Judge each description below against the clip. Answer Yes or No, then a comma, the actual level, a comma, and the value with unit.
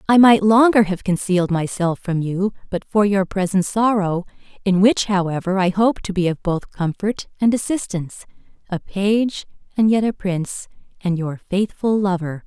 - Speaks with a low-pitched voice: No, high, 195 Hz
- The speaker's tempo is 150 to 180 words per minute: Yes, average, 165 wpm